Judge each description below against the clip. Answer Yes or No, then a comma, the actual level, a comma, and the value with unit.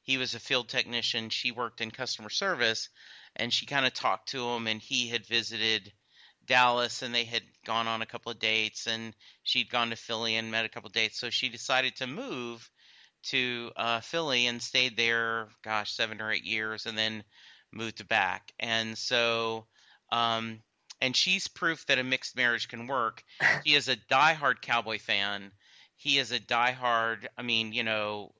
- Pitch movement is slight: Yes, narrow, 2.1 semitones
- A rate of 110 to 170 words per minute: No, average, 185 wpm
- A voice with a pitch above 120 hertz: No, low, 115 Hz